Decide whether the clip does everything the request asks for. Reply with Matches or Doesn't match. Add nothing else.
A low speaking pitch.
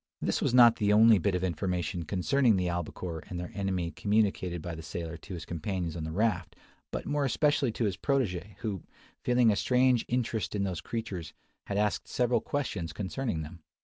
Matches